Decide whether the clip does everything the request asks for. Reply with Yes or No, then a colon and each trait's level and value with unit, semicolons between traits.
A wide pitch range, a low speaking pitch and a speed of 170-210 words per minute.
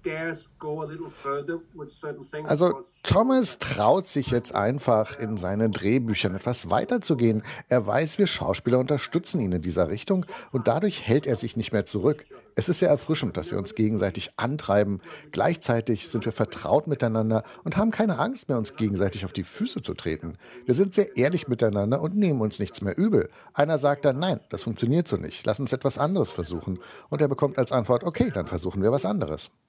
Yes: wide, 7.0 semitones; low, 130 Hz; average, 180 wpm